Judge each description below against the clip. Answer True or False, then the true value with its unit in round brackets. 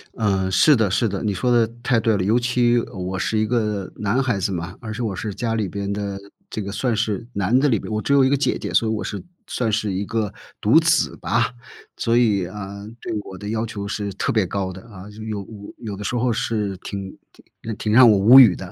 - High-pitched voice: False (105 Hz)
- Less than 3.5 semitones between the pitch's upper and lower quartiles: True (2.8 semitones)